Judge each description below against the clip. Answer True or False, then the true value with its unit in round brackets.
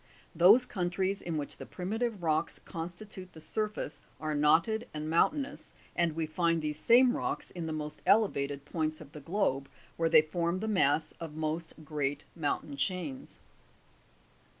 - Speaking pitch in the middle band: True (165 Hz)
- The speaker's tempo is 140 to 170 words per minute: True (155 wpm)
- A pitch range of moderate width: True (3.6 semitones)